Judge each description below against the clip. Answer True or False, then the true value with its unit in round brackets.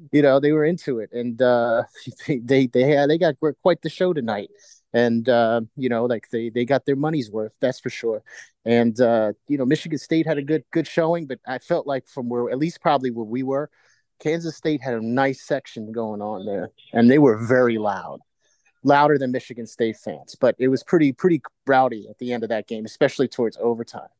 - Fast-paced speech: True (220 wpm)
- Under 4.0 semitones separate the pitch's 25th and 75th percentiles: False (4.7 semitones)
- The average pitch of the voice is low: True (130 Hz)